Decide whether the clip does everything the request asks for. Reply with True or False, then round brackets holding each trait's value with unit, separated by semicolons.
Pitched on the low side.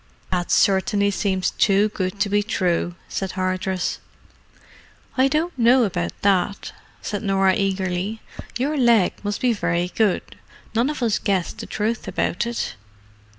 False (200 Hz)